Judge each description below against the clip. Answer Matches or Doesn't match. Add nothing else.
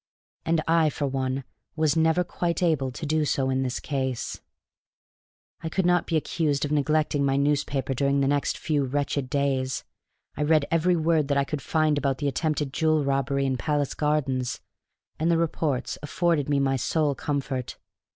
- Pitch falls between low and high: Matches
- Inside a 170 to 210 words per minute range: Matches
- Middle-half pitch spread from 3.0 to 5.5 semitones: Doesn't match